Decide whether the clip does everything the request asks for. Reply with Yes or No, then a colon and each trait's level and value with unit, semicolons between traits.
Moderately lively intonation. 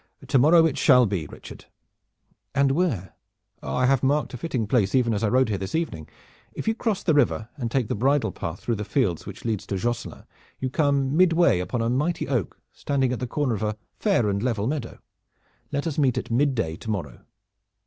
Yes: average, 4.9 semitones